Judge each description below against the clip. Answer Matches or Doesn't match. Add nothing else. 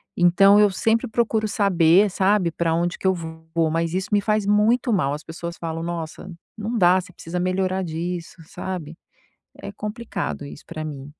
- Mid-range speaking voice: Matches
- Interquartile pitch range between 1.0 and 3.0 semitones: Doesn't match